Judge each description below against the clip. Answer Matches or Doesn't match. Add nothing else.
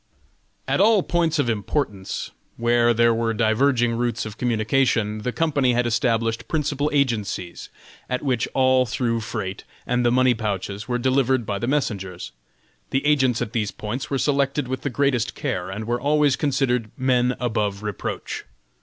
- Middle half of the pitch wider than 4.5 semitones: Doesn't match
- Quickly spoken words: Doesn't match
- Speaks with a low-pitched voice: Matches